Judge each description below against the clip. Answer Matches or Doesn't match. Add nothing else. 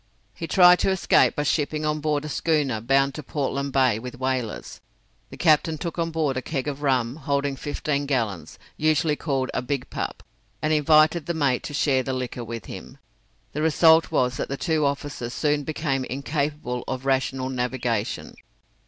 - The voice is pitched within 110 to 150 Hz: Matches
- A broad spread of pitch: Doesn't match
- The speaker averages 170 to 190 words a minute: Matches